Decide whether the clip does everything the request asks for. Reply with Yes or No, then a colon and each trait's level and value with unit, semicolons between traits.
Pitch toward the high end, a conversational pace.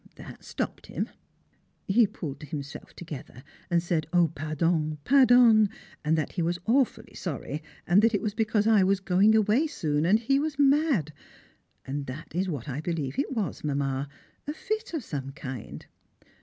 No: medium, 175 Hz; average, 170 wpm